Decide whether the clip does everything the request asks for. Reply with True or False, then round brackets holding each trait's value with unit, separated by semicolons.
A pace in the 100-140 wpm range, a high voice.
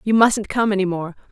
False (230 wpm; 200 Hz)